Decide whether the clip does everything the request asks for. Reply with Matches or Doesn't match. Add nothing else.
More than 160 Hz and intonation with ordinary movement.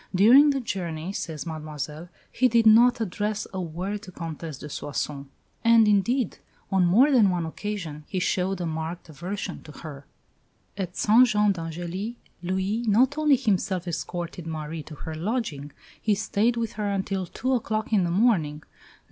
Matches